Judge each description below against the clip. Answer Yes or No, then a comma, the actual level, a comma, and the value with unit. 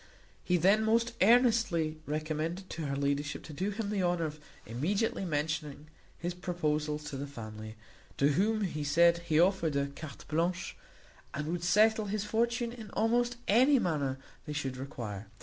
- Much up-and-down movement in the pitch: Yes, wide, 5.7 semitones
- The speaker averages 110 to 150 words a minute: No, average, 165 wpm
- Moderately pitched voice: Yes, medium, 170 Hz